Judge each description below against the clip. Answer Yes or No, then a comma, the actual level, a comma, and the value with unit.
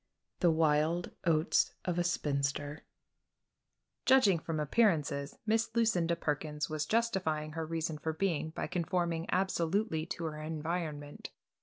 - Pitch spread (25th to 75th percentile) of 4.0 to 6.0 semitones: No, narrow, 2.6 semitones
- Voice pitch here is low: No, medium, 160 Hz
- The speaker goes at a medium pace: No, slow, 125 wpm